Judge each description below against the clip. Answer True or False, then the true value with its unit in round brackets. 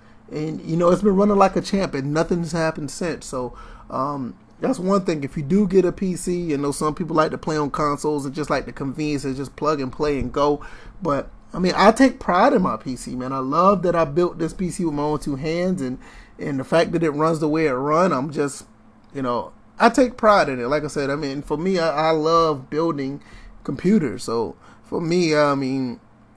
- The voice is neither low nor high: True (155 Hz)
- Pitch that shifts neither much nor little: True (4.0 semitones)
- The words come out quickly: True (235 wpm)